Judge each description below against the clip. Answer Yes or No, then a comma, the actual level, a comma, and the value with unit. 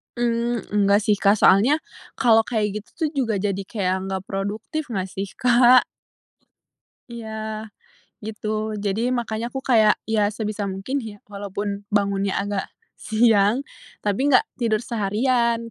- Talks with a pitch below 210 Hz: No, high, 215 Hz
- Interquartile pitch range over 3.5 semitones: No, average, 2.7 semitones